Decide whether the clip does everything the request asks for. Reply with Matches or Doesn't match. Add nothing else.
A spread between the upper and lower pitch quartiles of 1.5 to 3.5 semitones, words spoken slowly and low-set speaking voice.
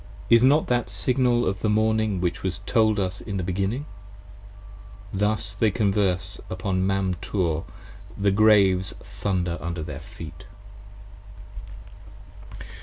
Matches